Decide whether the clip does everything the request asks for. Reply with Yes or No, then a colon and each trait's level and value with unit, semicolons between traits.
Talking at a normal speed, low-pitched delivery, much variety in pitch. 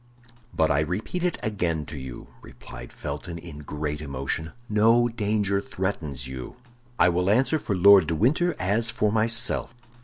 Yes: average, 155 wpm; very low, 95 Hz; wide, 6.2 semitones